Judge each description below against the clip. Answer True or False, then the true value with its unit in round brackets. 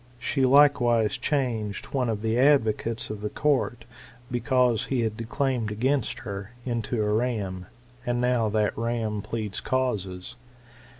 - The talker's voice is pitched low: True (115 Hz)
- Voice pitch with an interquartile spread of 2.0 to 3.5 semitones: True (2.9 semitones)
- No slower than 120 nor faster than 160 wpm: True (140 wpm)